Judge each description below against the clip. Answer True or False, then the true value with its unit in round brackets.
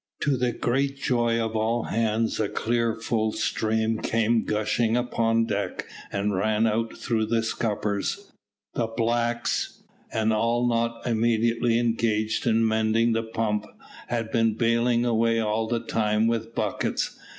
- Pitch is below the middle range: True (115 Hz)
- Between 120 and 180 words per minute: True (140 wpm)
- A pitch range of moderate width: False (1.1 semitones)